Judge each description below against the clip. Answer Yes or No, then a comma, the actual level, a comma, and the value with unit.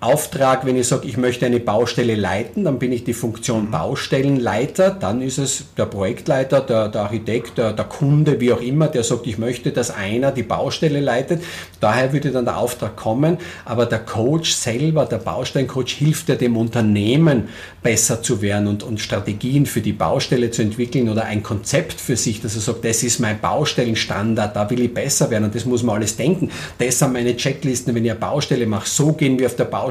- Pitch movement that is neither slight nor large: Yes, average, 3.5 semitones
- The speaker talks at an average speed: No, fast, 205 wpm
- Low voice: Yes, low, 120 Hz